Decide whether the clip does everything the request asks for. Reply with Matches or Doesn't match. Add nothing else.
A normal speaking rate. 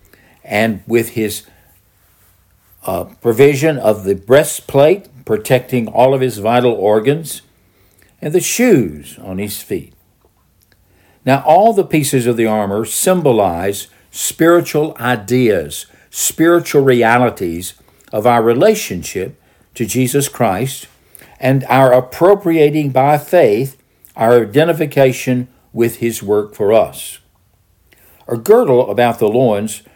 Doesn't match